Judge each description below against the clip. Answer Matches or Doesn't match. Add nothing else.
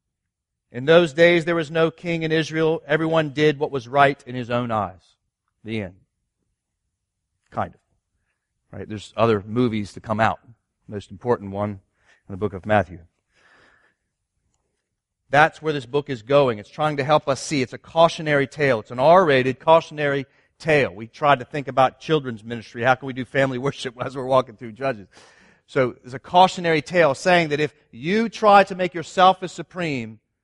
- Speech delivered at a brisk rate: Doesn't match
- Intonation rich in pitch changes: Matches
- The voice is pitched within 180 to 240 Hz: Doesn't match